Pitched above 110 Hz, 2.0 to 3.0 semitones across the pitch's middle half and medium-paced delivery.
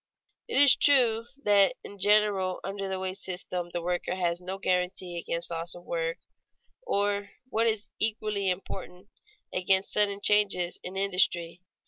Yes: high, 190 Hz; narrow, 2.4 semitones; average, 145 wpm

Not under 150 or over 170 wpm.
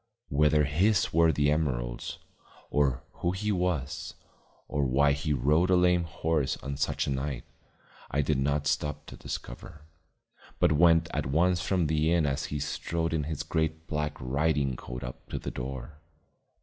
Yes: average, 165 wpm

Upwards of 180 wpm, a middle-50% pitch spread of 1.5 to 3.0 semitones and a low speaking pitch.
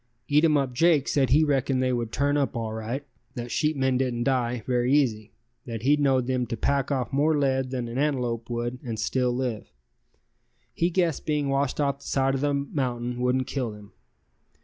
Yes: average, 190 wpm; average, 2.7 semitones; low, 130 Hz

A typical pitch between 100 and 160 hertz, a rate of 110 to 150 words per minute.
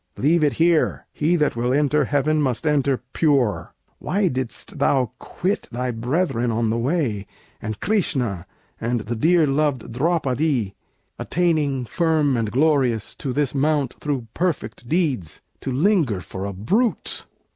Yes: low, 135 Hz; average, 145 wpm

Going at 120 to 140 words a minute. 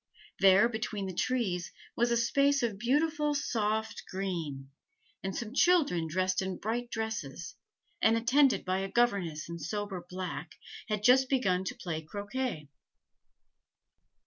Yes: slow, 135 wpm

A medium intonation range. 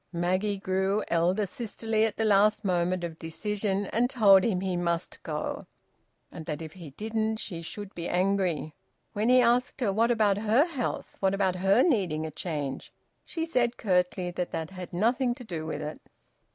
Yes: average, 4.1 semitones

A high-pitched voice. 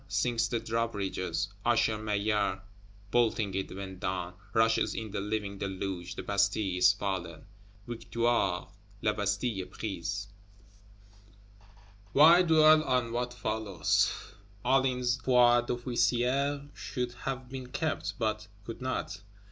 No: low, 110 Hz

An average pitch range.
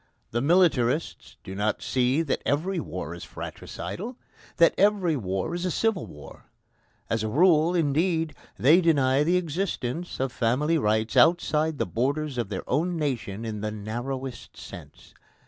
No: wide, 6.4 semitones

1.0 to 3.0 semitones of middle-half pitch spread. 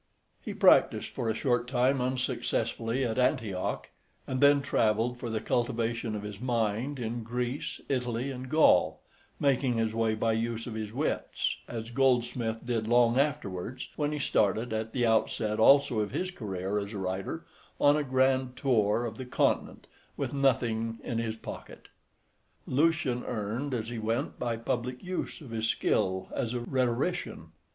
Yes: average, 2.7 semitones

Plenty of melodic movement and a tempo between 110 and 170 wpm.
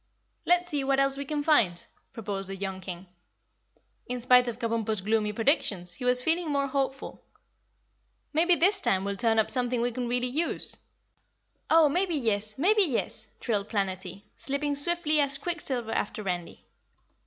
Yes: wide, 5.8 semitones; average, 160 wpm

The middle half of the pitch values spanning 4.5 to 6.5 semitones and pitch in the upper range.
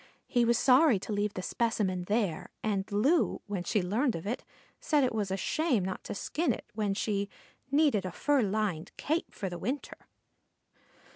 Yes: average, 4.9 semitones; high, 210 Hz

